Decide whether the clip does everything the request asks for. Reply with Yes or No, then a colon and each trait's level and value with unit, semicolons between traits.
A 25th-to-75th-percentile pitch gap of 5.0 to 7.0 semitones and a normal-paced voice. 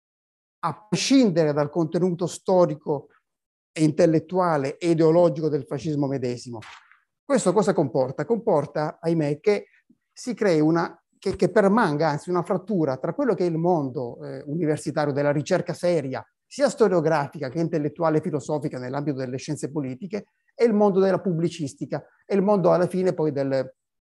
No: average, 3.7 semitones; average, 150 wpm